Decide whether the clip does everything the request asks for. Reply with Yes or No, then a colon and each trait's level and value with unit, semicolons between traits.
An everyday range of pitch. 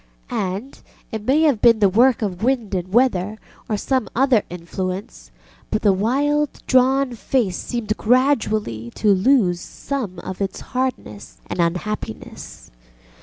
No: wide, 5.7 semitones